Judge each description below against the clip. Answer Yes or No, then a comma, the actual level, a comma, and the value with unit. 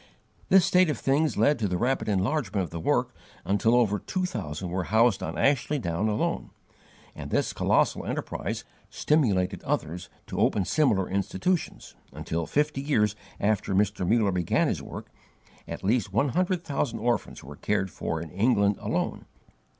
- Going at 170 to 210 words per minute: No, average, 160 wpm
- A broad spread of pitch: Yes, wide, 6.5 semitones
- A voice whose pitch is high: No, low, 105 Hz